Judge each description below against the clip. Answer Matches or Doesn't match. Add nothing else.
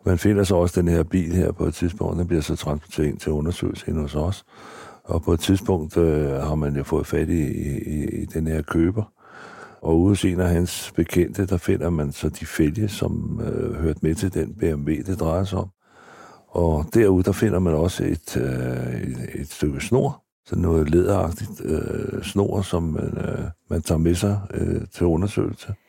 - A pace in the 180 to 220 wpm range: Matches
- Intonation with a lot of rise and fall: Doesn't match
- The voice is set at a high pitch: Doesn't match